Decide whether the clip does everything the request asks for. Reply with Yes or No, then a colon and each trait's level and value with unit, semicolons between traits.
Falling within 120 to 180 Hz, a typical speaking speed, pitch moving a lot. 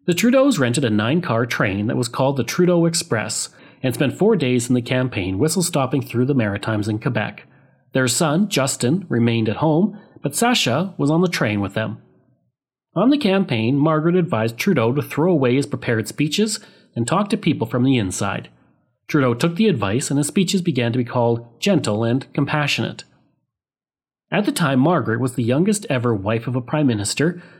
Yes: low, 135 Hz; average, 190 wpm; wide, 6.3 semitones